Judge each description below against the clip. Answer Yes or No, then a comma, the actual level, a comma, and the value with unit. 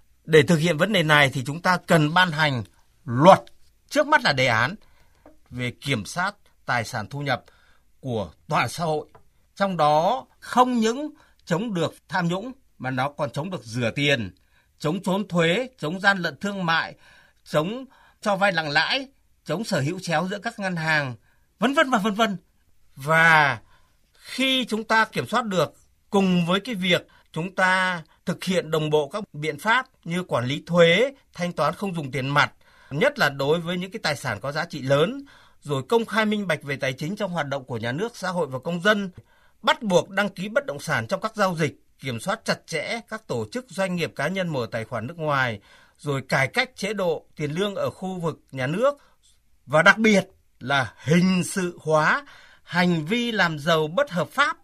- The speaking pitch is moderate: Yes, medium, 170 Hz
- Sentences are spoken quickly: No, average, 200 wpm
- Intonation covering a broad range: Yes, wide, 5.9 semitones